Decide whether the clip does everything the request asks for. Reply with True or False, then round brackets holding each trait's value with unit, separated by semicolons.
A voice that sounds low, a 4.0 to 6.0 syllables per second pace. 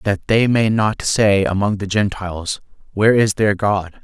True (100 Hz; 4.5 syllables/s)